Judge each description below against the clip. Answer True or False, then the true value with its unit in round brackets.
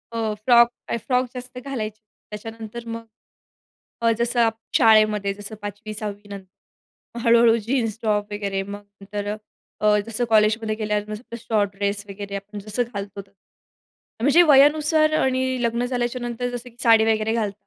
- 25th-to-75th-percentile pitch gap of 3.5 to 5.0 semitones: False (2.5 semitones)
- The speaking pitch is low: False (220 Hz)